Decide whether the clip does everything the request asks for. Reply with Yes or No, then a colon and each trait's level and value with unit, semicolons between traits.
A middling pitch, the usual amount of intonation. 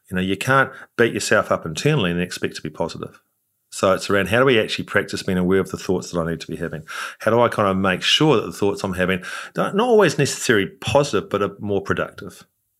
No: very low, 95 Hz; average, 4.3 semitones